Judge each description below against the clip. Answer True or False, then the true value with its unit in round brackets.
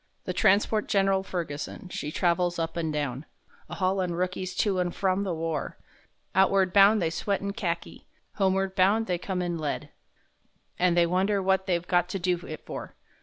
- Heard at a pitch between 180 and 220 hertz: True (185 Hz)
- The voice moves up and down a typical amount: False (2.2 semitones)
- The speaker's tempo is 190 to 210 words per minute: False (175 wpm)